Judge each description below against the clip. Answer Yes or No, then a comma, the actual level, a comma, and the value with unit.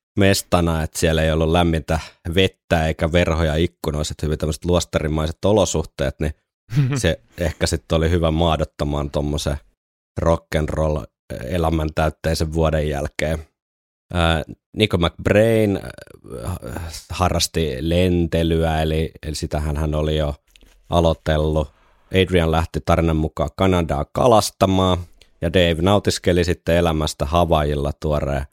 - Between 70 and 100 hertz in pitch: Yes, very low, 80 Hz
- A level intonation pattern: Yes, narrow, 2.2 semitones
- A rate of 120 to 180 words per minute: No, average, 105 wpm